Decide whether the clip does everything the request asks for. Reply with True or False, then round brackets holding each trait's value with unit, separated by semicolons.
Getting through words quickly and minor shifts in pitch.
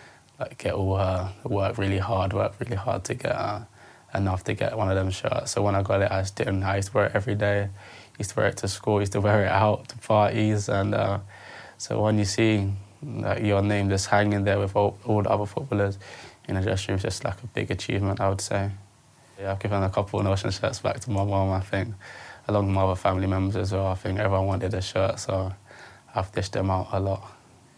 True (245 wpm; 1.4 semitones)